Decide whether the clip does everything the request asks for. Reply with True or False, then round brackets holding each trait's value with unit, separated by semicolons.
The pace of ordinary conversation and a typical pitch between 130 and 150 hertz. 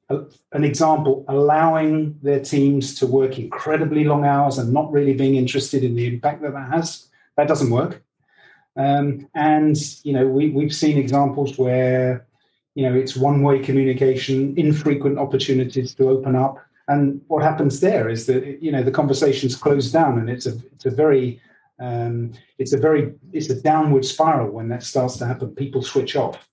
True (175 wpm; 140 Hz)